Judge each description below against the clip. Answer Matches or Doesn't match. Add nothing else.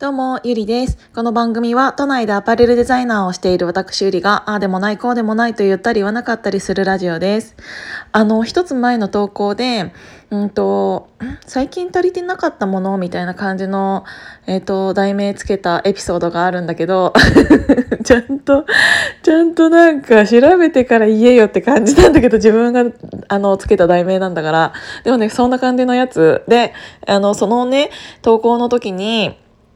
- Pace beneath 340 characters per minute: Doesn't match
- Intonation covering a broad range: Doesn't match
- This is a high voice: Matches